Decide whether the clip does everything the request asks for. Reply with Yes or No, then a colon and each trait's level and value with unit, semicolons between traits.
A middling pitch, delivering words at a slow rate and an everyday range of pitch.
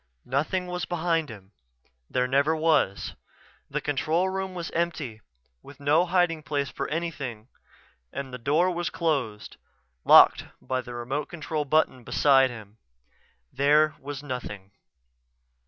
Yes: medium, 145 Hz; slow, 130 wpm; average, 4.5 semitones